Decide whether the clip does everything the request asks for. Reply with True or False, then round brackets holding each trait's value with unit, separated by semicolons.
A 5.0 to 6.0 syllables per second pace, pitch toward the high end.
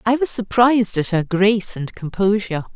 True (5.5 syllables/s; 205 Hz)